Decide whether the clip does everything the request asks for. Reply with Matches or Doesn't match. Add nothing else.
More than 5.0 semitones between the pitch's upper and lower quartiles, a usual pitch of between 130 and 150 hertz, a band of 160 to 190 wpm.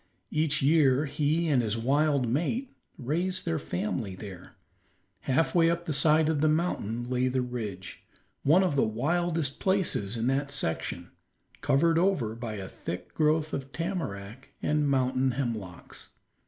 Doesn't match